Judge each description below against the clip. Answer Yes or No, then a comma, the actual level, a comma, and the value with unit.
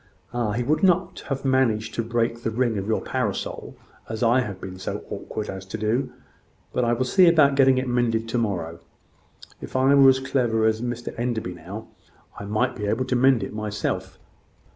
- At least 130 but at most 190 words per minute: No, average, 200 wpm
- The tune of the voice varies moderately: Yes, average, 3.3 semitones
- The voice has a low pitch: Yes, low, 120 Hz